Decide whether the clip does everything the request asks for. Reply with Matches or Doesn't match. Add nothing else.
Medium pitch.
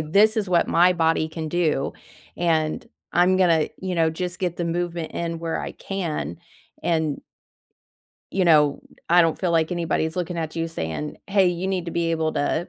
Matches